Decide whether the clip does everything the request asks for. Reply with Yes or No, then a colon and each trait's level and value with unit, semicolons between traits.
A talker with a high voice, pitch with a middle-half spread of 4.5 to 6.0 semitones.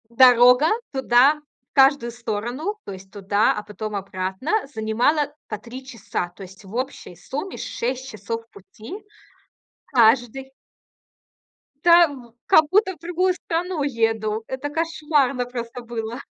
Yes: high, 245 Hz; average, 4.8 semitones